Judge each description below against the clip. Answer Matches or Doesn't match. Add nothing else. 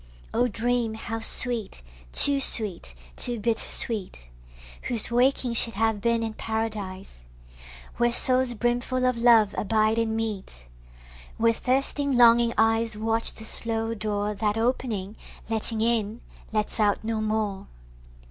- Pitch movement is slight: Matches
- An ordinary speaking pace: Doesn't match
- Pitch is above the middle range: Matches